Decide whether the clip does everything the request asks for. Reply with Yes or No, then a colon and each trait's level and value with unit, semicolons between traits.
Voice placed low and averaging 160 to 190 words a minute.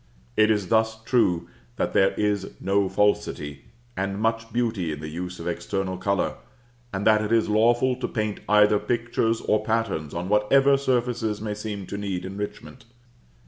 Yes: low, 105 Hz; average, 165 wpm